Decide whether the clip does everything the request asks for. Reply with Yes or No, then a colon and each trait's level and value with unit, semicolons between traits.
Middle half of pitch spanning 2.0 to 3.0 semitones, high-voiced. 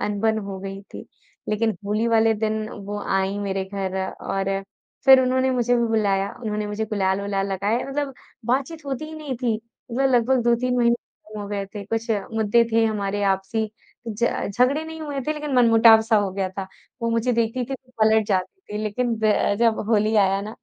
No: average, 3.4 semitones; high, 220 Hz